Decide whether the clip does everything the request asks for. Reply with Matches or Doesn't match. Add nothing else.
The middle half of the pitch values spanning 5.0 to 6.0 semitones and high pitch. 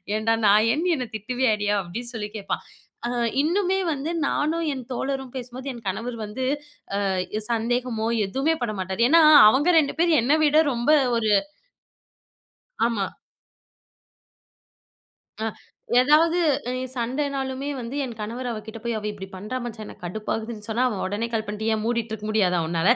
Doesn't match